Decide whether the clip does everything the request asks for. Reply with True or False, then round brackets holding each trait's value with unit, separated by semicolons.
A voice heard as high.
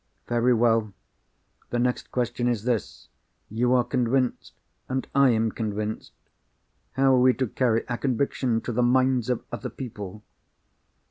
False (120 Hz)